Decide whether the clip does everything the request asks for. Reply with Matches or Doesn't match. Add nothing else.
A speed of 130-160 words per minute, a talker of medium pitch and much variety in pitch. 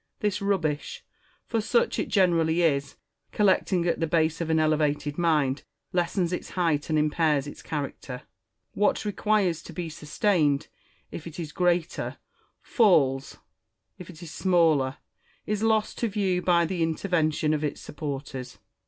Doesn't match